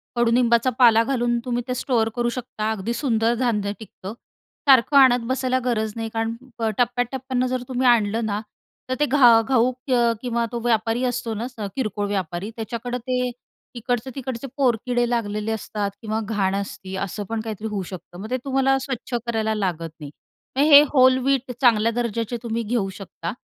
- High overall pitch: Yes, high, 235 Hz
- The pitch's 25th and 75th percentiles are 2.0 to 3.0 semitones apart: Yes, narrow, 2.5 semitones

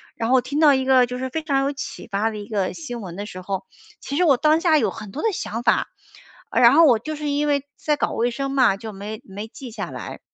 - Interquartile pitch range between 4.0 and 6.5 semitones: Yes, average, 5.0 semitones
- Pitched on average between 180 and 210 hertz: No, very high, 255 Hz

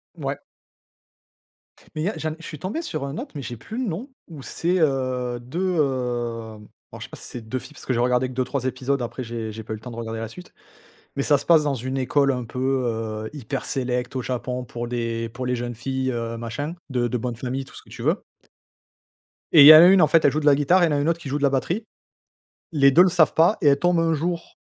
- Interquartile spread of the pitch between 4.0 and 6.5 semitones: Yes, average, 4.3 semitones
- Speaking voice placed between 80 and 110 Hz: No, low, 130 Hz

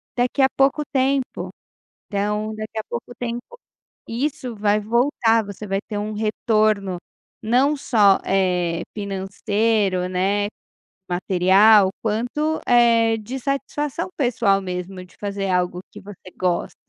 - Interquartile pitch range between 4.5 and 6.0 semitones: No, average, 3.7 semitones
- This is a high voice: Yes, high, 215 Hz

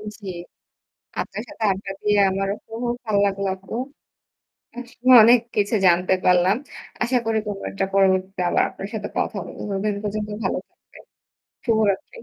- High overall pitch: Yes, high, 200 Hz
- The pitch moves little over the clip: Yes, narrow, 2.2 semitones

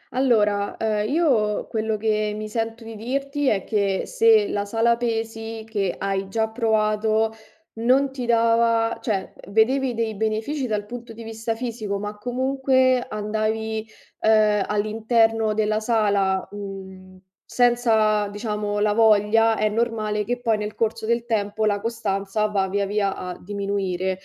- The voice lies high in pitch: Yes, high, 220 Hz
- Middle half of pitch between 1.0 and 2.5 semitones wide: Yes, narrow, 1.8 semitones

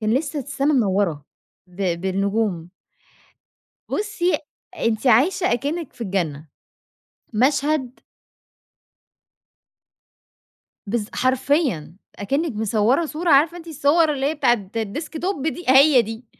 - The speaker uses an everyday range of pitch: No, wide, 6.7 semitones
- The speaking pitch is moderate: No, very high, 260 Hz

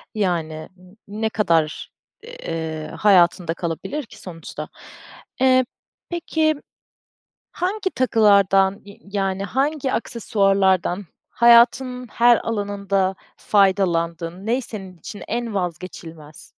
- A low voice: No, high, 200 Hz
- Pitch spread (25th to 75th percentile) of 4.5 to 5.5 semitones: Yes, average, 5.0 semitones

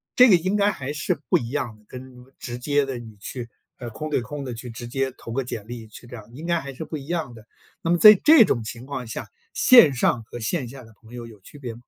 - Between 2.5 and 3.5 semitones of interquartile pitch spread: No, average, 4.4 semitones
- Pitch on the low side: Yes, low, 130 Hz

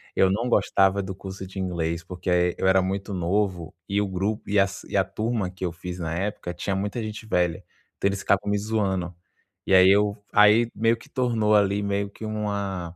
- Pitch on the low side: Yes, low, 100 Hz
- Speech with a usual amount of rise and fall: No, narrow, 2.3 semitones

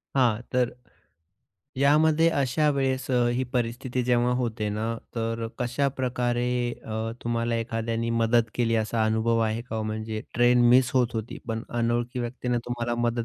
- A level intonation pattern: Yes, narrow, 1.7 semitones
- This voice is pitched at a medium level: No, low, 120 Hz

